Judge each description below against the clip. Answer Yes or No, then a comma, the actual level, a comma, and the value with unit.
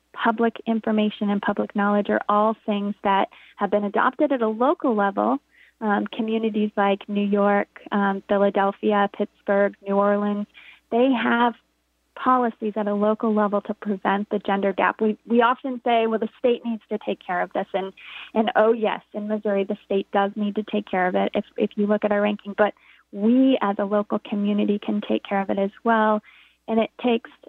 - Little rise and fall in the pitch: Yes, narrow, 1.8 semitones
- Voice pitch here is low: No, high, 210 Hz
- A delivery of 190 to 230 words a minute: Yes, average, 195 wpm